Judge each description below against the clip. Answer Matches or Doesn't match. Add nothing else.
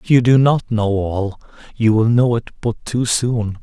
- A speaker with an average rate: Doesn't match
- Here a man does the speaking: Matches